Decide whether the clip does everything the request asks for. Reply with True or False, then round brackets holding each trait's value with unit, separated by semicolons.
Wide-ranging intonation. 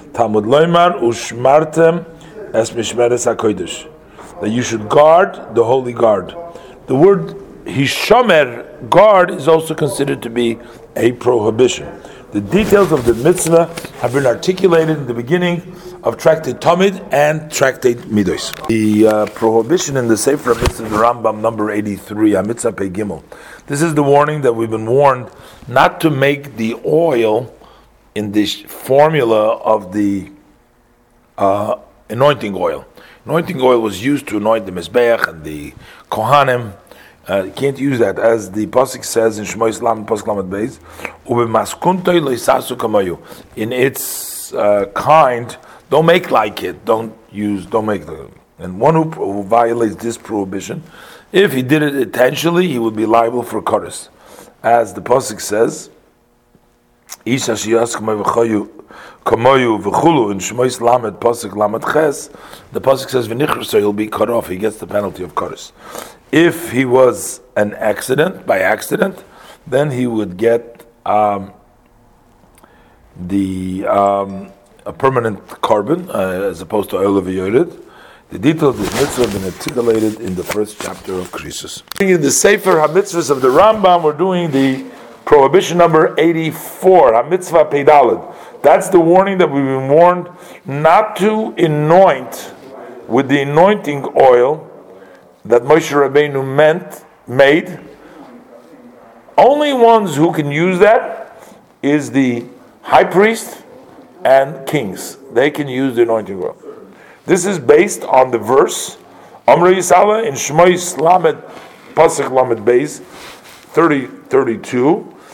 True (6.4 semitones)